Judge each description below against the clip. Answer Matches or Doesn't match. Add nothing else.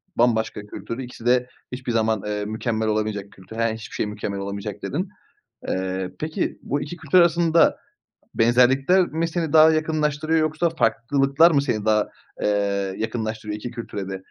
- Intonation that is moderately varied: Doesn't match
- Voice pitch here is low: Matches